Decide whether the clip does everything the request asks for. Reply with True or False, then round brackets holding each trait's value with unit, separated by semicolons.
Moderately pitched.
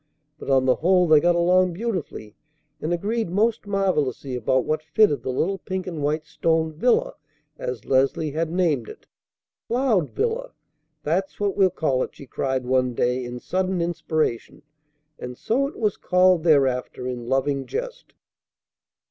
True (160 Hz)